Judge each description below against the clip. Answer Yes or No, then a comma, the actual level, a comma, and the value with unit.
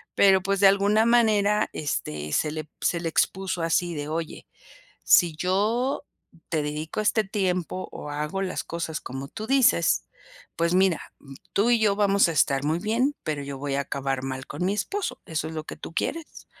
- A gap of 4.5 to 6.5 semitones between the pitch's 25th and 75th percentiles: Yes, average, 5.3 semitones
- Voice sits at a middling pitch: Yes, medium, 180 Hz